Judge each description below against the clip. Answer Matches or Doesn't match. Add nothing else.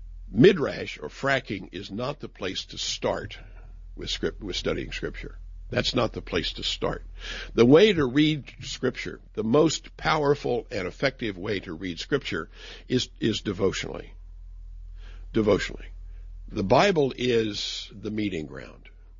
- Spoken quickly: Doesn't match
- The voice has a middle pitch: Doesn't match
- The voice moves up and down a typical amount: Doesn't match